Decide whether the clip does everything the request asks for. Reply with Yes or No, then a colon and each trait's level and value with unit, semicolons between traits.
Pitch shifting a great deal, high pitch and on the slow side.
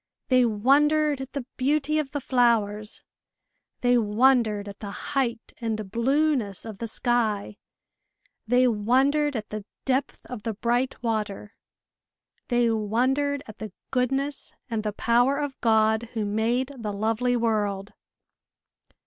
No: average, 3.7 semitones; high, 235 Hz; slow, 130 wpm